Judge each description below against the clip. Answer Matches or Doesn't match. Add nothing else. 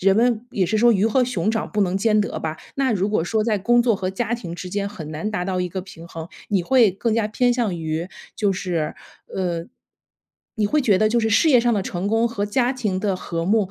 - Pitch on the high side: Matches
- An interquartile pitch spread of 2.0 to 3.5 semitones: Doesn't match